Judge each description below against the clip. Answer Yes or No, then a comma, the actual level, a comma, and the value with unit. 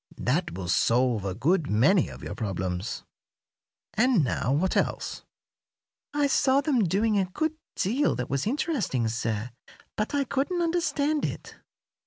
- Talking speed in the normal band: Yes, average, 145 wpm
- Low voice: No, medium, 185 Hz